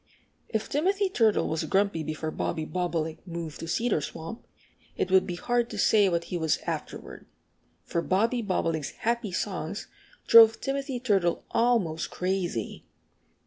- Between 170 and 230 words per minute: No, average, 145 wpm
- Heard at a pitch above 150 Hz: Yes, high, 190 Hz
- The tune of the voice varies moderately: No, wide, 5.8 semitones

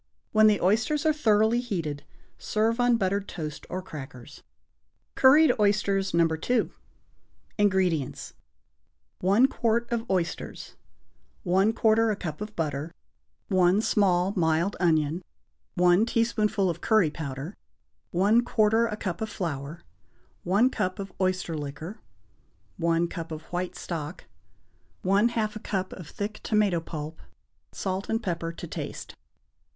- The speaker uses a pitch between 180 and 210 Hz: Yes, high, 190 Hz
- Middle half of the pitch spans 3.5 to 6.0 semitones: Yes, average, 4.5 semitones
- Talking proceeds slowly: Yes, slow, 125 wpm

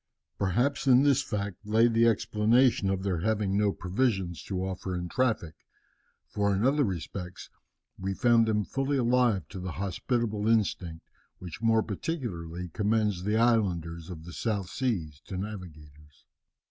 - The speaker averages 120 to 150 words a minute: Yes, average, 145 wpm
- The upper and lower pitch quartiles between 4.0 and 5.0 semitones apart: Yes, average, 4.3 semitones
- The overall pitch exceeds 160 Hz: No, low, 100 Hz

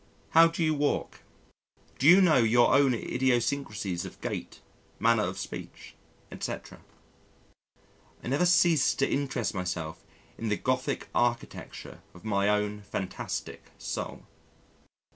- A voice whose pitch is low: Yes, low, 120 Hz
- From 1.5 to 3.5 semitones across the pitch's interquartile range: No, wide, 5.4 semitones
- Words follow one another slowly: Yes, slow, 125 wpm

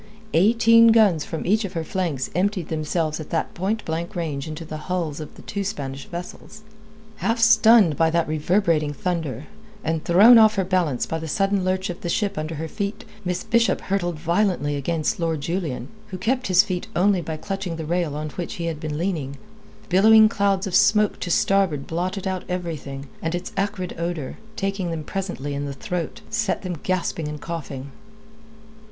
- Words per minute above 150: Yes, average, 185 wpm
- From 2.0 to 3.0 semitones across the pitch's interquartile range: No, average, 4.0 semitones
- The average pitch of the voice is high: No, medium, 175 Hz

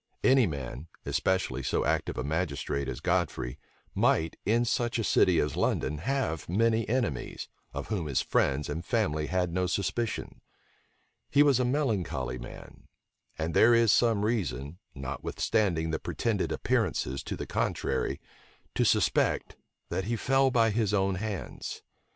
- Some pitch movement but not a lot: No, wide, 7.5 semitones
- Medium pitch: No, very low, 95 Hz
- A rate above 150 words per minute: No, average, 145 wpm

